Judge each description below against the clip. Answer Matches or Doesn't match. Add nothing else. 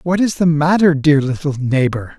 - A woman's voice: Doesn't match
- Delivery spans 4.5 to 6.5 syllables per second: Matches